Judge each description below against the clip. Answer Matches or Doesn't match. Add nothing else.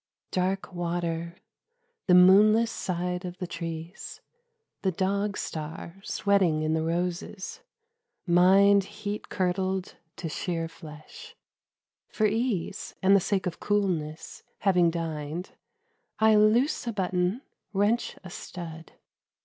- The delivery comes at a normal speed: Doesn't match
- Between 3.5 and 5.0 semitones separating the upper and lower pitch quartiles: Doesn't match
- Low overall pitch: Doesn't match